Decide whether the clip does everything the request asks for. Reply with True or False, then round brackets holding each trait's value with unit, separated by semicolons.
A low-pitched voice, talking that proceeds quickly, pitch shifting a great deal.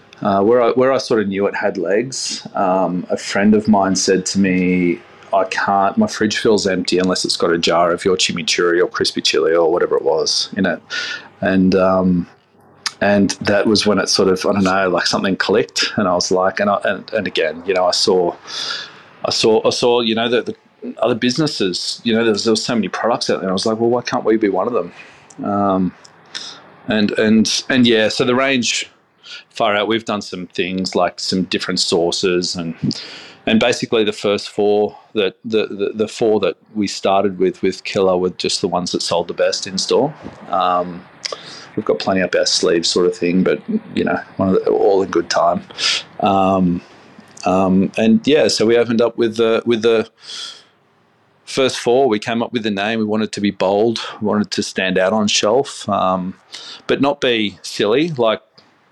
False (105 Hz; 210 wpm; 4.2 semitones)